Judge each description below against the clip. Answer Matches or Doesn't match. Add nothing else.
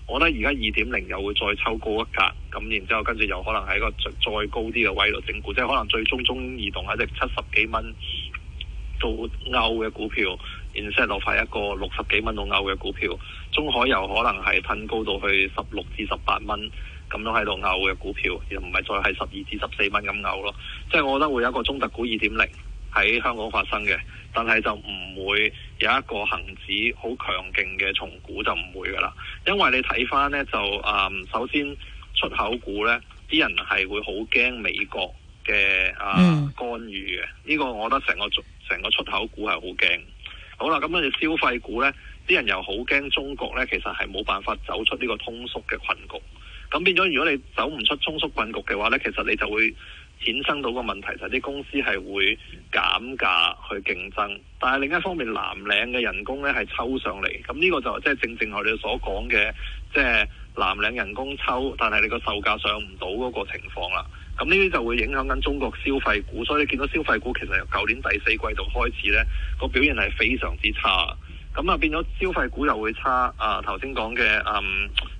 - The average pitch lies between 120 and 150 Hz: Doesn't match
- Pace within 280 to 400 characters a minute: Matches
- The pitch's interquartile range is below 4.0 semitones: Doesn't match